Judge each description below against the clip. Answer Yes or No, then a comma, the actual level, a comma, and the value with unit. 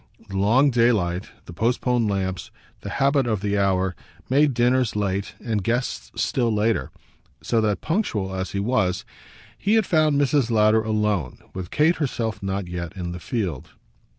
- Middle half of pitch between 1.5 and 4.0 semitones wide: No, average, 4.6 semitones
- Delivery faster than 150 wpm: Yes, average, 160 wpm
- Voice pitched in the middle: No, low, 110 Hz